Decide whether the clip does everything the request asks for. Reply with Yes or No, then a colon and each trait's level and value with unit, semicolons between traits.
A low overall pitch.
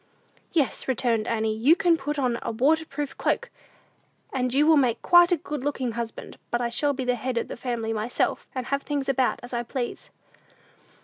No: very high, 255 Hz